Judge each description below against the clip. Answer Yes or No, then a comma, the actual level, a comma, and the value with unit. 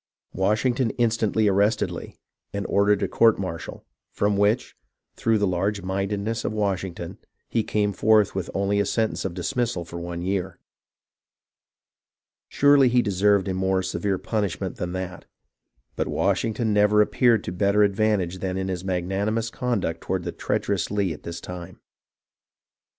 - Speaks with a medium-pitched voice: No, low, 100 Hz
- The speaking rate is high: No, average, 155 wpm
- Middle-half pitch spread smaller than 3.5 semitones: Yes, narrow, 2.6 semitones